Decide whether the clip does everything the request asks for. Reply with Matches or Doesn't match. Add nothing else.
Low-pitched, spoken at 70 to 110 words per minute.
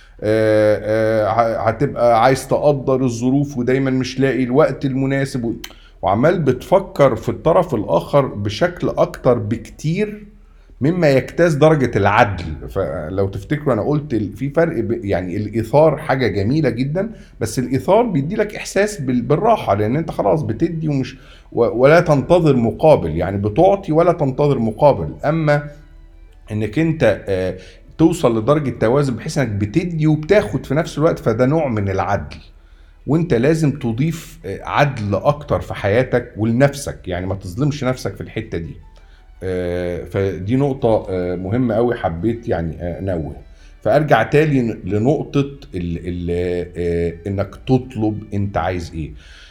Doesn't match